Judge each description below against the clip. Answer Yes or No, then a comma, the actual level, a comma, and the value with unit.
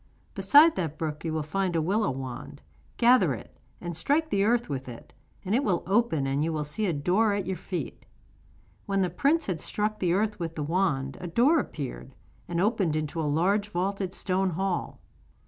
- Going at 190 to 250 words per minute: Yes, average, 200 wpm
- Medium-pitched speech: Yes, medium, 180 Hz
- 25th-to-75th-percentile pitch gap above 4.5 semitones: Yes, average, 4.9 semitones